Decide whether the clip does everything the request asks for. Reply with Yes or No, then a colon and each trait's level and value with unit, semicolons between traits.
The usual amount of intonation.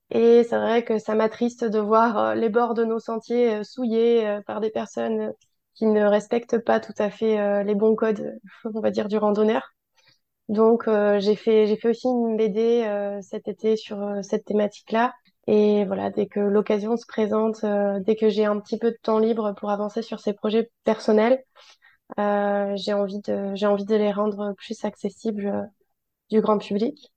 No: narrow, 1.7 semitones